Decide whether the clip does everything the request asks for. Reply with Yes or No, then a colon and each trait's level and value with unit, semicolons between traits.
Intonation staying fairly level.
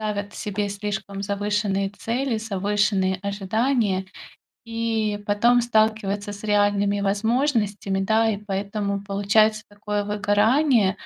Yes: narrow, 1.5 semitones